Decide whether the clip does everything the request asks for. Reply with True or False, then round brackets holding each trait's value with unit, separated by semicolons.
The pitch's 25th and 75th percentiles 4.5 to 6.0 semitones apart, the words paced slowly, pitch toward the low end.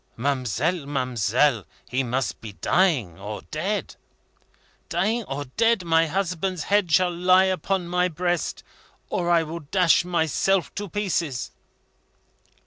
False (5.1 semitones; 125 wpm; 170 Hz)